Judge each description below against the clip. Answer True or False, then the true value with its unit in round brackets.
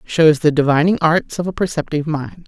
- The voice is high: False (160 Hz)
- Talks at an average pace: True (195 wpm)